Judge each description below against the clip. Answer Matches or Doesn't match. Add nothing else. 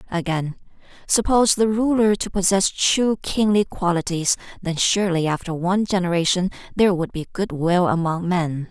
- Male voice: Doesn't match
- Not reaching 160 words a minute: Matches